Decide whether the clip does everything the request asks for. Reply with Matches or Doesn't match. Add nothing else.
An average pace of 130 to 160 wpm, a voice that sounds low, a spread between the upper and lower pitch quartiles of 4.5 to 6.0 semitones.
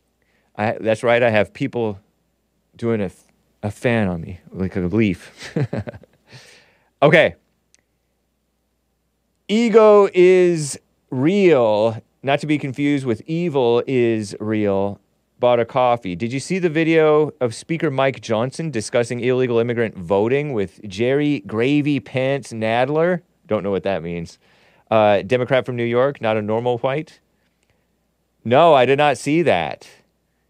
Matches